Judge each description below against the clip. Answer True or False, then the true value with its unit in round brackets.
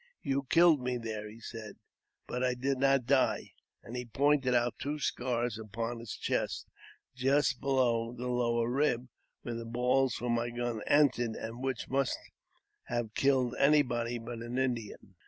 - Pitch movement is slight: True (2.3 semitones)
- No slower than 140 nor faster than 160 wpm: False (170 wpm)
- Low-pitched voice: True (125 Hz)